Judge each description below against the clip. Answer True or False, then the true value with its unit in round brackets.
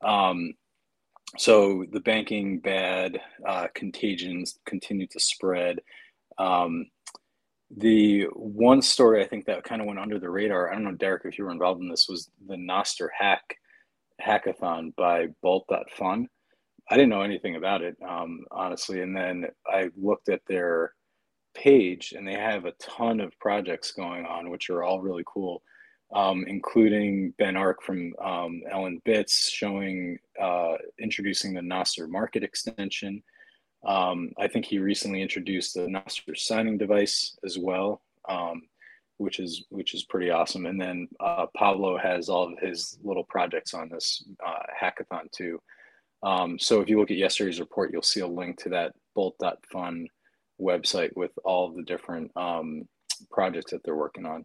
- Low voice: True (95 Hz)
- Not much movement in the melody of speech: True (2.2 semitones)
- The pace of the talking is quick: False (160 wpm)